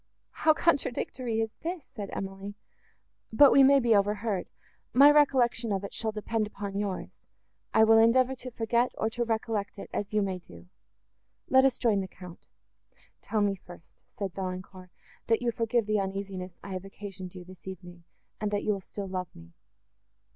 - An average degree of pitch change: Yes, average, 3.4 semitones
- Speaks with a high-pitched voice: Yes, high, 205 Hz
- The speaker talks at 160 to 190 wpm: Yes, average, 170 wpm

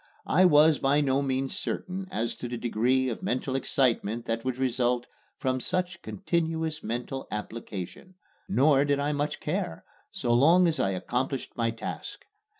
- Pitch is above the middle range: No, low, 135 Hz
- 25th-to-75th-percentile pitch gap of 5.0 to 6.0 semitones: No, average, 4.5 semitones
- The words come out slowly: No, average, 155 wpm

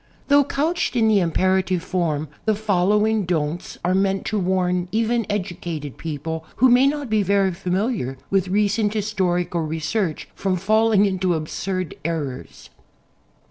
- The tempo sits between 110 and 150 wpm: Yes, average, 140 wpm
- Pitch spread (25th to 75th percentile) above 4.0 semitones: No, average, 3.7 semitones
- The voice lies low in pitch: No, high, 190 Hz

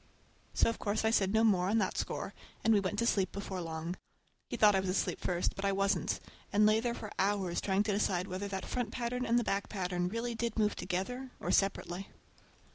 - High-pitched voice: Yes, high, 200 Hz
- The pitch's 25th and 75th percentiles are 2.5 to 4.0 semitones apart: Yes, average, 2.8 semitones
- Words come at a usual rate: No, fast, 220 wpm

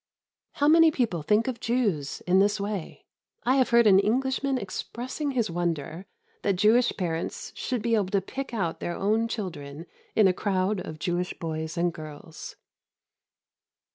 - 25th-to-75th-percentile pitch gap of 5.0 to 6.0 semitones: Yes, wide, 5.5 semitones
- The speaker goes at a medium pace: Yes, average, 160 wpm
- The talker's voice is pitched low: No, high, 200 Hz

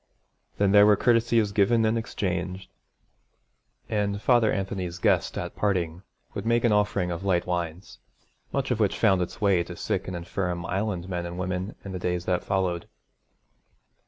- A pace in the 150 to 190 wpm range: Yes, average, 165 wpm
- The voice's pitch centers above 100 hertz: No, very low, 95 Hz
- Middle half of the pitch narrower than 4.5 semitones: Yes, average, 2.9 semitones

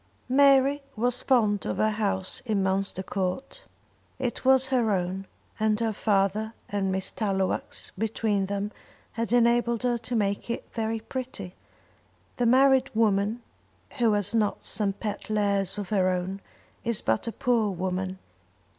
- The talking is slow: No, average, 145 wpm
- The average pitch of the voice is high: Yes, high, 215 Hz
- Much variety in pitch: No, average, 3.3 semitones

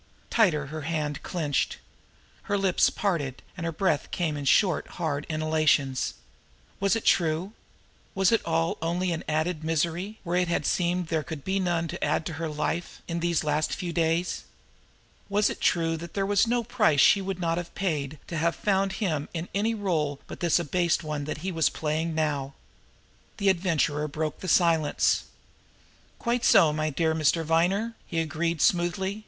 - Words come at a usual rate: Yes, average, 175 wpm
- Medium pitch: Yes, medium, 165 Hz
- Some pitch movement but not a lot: Yes, average, 3.1 semitones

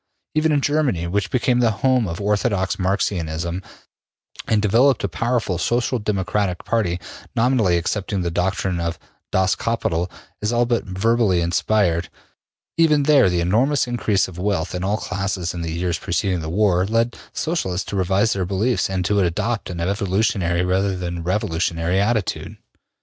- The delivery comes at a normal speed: Yes, average, 160 wpm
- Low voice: Yes, very low, 95 Hz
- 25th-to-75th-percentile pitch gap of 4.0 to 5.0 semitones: Yes, average, 4.3 semitones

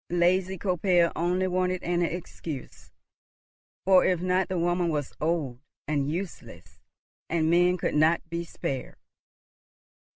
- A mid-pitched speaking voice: Yes, medium, 175 Hz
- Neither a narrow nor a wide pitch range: No, narrow, 2.0 semitones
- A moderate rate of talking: No, slow, 125 wpm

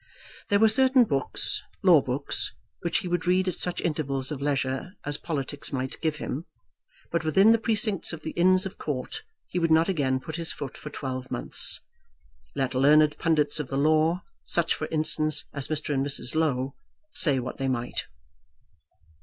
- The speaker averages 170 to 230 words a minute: Yes, average, 180 wpm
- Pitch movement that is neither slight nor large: Yes, average, 4.1 semitones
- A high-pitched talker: No, medium, 155 Hz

